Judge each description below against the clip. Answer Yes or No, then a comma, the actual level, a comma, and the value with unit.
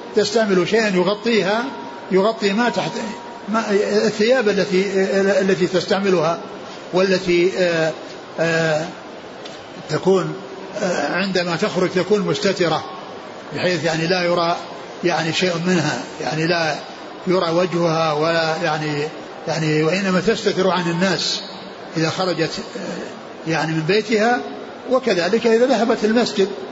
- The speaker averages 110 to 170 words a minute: No, average, 100 wpm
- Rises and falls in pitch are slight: No, average, 3.7 semitones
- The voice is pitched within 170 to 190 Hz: Yes, medium, 185 Hz